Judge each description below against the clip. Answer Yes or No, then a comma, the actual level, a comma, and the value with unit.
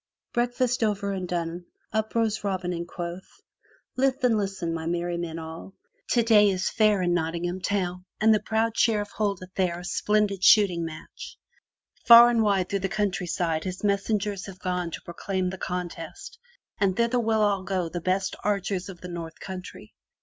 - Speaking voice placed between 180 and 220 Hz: Yes, high, 190 Hz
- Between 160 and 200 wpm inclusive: Yes, average, 185 wpm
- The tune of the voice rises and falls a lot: No, average, 3.3 semitones